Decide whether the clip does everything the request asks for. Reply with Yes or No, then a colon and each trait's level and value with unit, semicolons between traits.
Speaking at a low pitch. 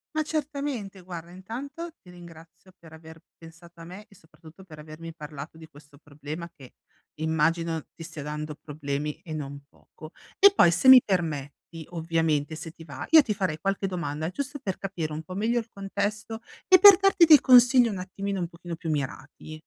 No: medium, 170 Hz